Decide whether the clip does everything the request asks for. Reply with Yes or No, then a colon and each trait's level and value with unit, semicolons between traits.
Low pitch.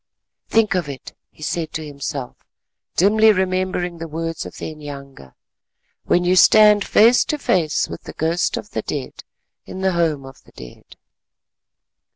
No: medium, 170 Hz